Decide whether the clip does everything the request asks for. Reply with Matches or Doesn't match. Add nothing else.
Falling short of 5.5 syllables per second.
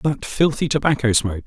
Doesn't match